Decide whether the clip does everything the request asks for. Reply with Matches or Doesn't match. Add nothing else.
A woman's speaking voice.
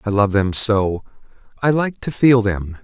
Doesn't match